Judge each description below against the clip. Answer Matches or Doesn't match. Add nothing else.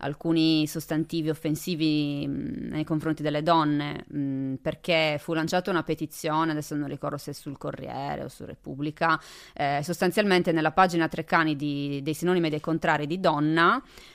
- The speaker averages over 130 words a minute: Matches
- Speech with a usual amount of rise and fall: Doesn't match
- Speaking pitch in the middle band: Matches